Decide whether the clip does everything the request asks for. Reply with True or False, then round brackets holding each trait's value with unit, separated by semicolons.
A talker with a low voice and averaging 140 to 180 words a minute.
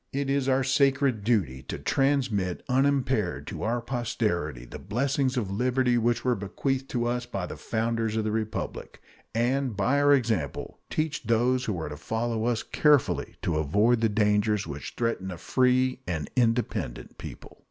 True (115 Hz; 165 wpm)